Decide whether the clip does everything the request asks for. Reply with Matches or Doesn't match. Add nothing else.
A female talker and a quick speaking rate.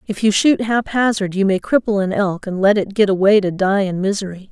Matches